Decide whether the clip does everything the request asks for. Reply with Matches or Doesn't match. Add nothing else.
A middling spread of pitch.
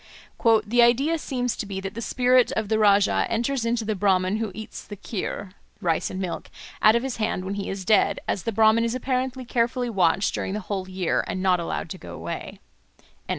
Matches